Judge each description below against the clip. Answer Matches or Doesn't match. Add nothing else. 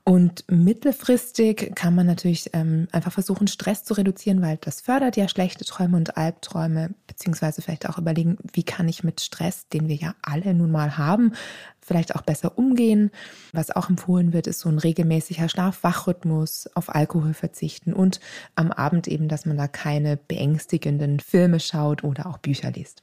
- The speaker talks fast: Doesn't match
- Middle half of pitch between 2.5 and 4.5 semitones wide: Matches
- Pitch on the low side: Doesn't match